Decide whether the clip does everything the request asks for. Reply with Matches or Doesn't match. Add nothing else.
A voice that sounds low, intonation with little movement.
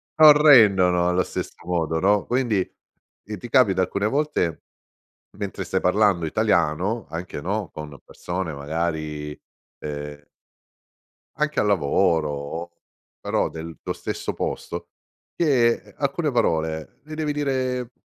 Doesn't match